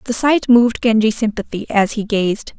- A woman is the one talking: Yes, female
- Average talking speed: Yes, average, 185 wpm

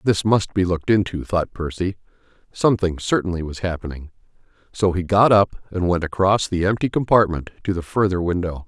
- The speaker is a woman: No, male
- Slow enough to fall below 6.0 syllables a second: Yes, 5.5 syllables/s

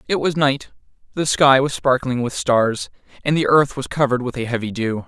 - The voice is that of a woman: No, male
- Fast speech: Yes, fast, 215 wpm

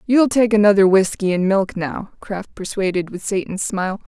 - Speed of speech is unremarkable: Yes, average, 175 wpm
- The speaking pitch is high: Yes, high, 200 Hz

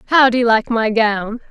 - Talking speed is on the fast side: Yes, fast, 240 wpm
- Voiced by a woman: Yes, female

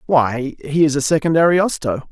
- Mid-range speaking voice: Yes, medium, 145 Hz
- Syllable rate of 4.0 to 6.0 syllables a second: Yes, 5.0 syllables/s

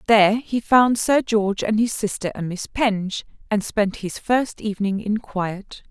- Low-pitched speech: No, high, 210 Hz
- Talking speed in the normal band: Yes, average, 185 wpm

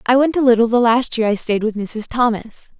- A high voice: Yes, high, 235 Hz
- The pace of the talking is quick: Yes, fast, 255 wpm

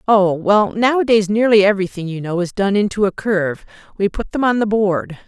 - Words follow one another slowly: No, fast, 205 wpm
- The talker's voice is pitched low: No, high, 200 Hz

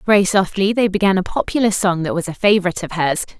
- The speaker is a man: No, female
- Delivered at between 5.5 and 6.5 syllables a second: No, 6.7 syllables/s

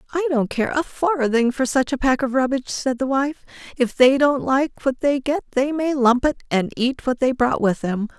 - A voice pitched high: Yes, very high, 265 Hz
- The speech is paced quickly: Yes, fast, 235 wpm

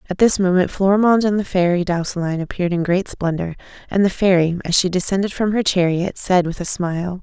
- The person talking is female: Yes, female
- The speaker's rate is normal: No, fast, 210 wpm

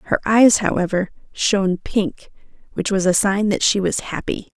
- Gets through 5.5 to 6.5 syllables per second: No, 4.7 syllables/s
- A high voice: Yes, high, 200 Hz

